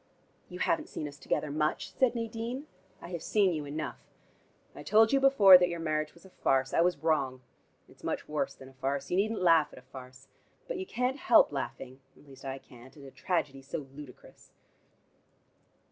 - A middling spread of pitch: No, wide, 7.3 semitones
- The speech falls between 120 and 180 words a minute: No, average, 195 wpm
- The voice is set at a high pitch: No, medium, 155 Hz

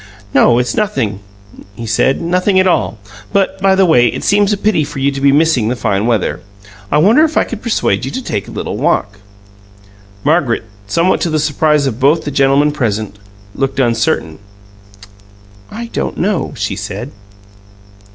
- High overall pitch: No, medium, 145 Hz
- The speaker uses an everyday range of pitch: No, wide, 7.7 semitones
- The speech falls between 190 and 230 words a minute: No, average, 175 wpm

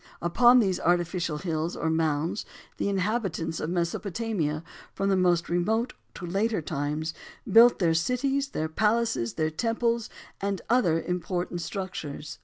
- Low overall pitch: No, medium, 175 Hz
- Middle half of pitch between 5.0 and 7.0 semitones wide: Yes, wide, 5.4 semitones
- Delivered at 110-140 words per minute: Yes, slow, 135 wpm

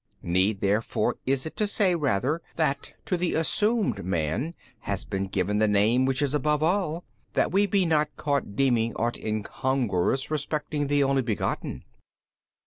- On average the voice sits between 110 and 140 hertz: Yes, low, 135 Hz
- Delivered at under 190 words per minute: Yes, average, 155 wpm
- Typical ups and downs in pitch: No, wide, 6.6 semitones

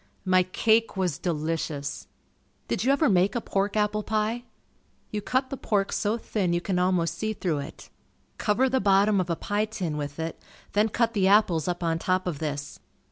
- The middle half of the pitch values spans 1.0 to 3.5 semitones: No, average, 4.2 semitones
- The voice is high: Yes, high, 195 Hz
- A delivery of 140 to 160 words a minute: No, average, 190 wpm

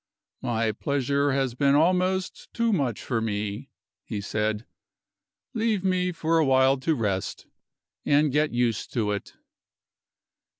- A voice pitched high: No, low, 135 Hz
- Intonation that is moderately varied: No, wide, 6.3 semitones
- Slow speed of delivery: Yes, slow, 130 wpm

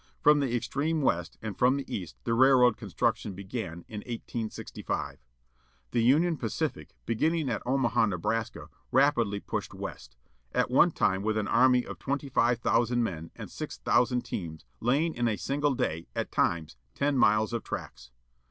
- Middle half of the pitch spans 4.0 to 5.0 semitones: Yes, average, 4.6 semitones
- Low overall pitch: Yes, low, 120 Hz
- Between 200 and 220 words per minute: No, average, 160 wpm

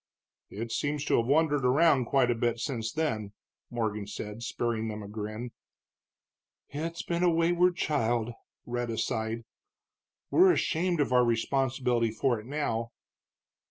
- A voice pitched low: Yes, low, 120 Hz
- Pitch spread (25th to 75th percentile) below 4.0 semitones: No, average, 4.7 semitones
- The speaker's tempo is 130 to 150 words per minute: Yes, average, 140 wpm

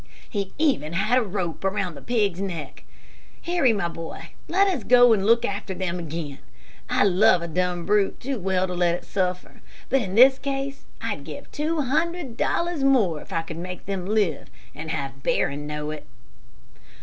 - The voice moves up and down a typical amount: No, wide, 6.6 semitones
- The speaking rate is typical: Yes, average, 185 wpm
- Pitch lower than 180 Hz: No, high, 195 Hz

